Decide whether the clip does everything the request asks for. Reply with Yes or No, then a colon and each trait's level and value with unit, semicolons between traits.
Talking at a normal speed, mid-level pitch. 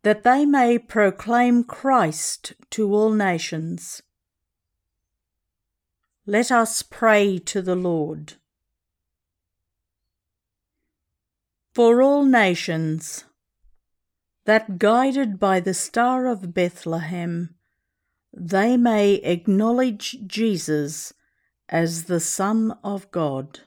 No: slow, 85 wpm; medium, 180 Hz